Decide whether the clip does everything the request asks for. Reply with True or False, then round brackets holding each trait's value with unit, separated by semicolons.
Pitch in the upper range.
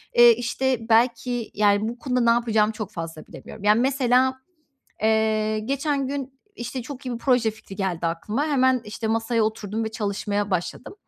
True (225 Hz)